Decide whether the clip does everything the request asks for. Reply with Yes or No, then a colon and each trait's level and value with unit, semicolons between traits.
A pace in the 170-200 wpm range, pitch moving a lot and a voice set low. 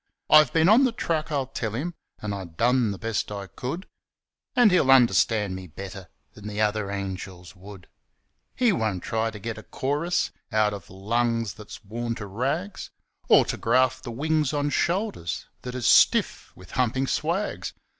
Yes: average, 175 wpm; wide, 6.3 semitones; low, 115 Hz